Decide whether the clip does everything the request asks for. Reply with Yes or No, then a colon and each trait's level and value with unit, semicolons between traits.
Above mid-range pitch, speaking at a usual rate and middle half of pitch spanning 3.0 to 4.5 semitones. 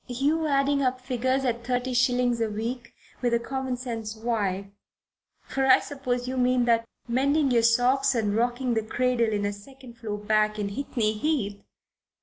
No: high, 245 Hz; average, 170 wpm; narrow, 2.6 semitones